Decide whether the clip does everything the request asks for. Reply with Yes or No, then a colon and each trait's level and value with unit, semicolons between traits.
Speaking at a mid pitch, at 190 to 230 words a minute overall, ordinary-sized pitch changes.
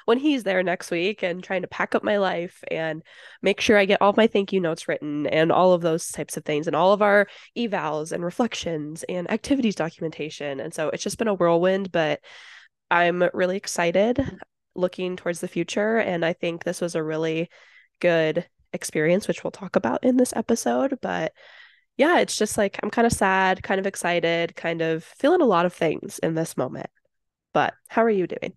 Yes: medium, 180 Hz; fast, 205 wpm; average, 3.6 semitones